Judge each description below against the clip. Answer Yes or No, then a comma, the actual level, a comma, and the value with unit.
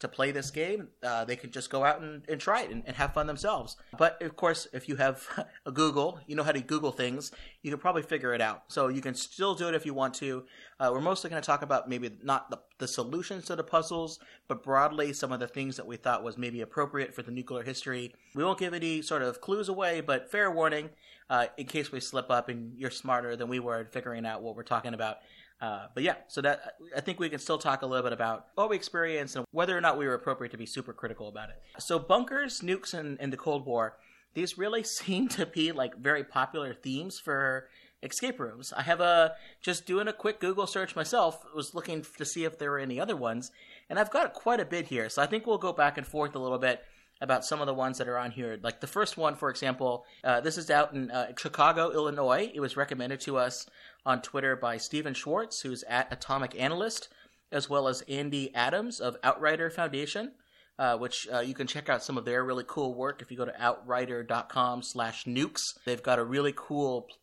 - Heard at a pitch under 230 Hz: Yes, medium, 140 Hz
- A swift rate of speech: Yes, fast, 240 wpm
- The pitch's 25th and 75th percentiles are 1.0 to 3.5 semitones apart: No, average, 4.6 semitones